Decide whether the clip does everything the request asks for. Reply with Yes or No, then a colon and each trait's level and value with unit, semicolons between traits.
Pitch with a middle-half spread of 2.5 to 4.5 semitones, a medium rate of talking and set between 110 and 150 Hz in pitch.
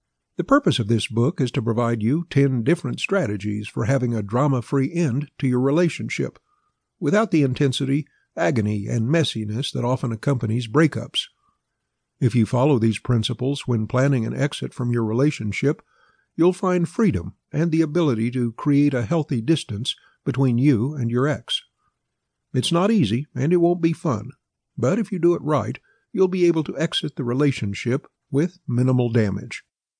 No: average, 5.3 semitones; average, 165 wpm; low, 135 Hz